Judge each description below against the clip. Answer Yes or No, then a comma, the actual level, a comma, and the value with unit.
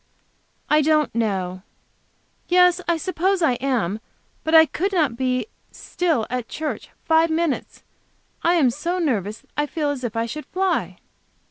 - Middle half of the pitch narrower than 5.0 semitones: No, wide, 5.6 semitones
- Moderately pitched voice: No, very high, 300 Hz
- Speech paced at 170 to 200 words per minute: No, average, 150 wpm